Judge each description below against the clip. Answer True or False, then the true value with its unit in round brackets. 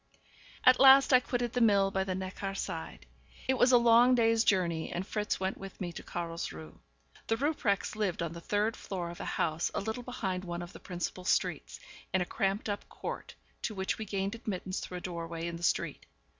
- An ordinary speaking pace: False (210 wpm)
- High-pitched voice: True (195 Hz)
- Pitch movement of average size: True (4.3 semitones)